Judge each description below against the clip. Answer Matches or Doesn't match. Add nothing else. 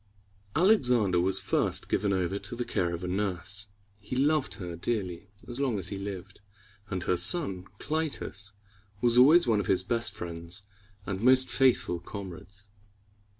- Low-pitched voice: Matches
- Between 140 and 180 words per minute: Matches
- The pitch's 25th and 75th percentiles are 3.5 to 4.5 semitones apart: Doesn't match